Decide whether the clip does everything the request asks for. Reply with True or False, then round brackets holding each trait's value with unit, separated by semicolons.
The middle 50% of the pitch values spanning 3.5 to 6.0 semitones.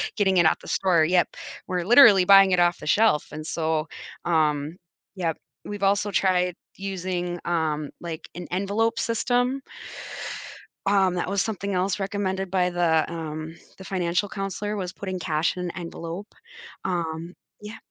False (2.7 semitones)